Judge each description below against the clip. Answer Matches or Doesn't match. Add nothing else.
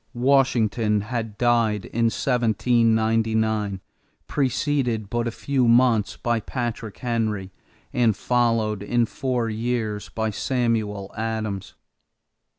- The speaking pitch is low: Matches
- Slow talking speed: Matches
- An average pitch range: Doesn't match